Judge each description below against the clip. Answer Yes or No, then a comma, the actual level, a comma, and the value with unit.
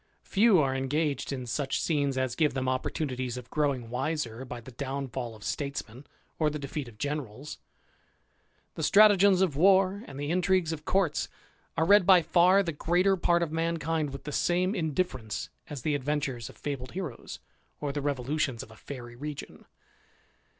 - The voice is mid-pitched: Yes, medium, 145 Hz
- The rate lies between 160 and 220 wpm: Yes, average, 170 wpm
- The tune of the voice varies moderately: Yes, average, 4.6 semitones